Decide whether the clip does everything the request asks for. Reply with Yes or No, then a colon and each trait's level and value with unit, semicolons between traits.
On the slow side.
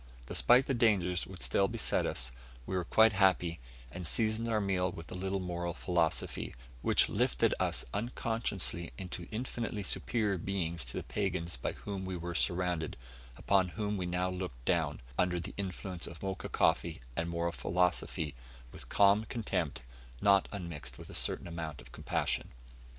No: average, 160 wpm